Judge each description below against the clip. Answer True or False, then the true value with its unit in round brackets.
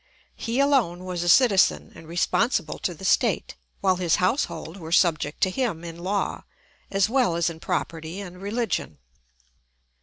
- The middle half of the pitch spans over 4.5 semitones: False (4.0 semitones)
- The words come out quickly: False (155 wpm)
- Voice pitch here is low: False (185 Hz)